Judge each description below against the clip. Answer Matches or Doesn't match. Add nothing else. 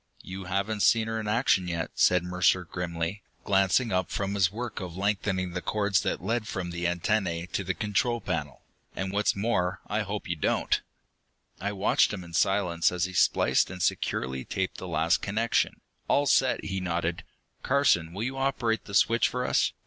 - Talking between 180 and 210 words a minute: Matches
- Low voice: Matches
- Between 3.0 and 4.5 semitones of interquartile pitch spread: Matches